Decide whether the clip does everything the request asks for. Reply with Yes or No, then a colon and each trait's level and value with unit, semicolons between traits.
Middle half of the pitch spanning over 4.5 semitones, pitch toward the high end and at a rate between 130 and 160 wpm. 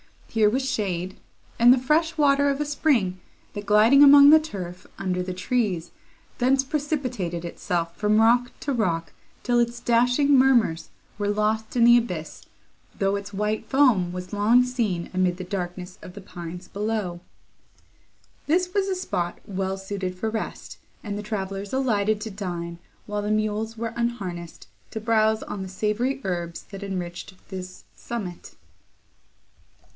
Yes: average, 4.9 semitones; high, 210 Hz; average, 155 wpm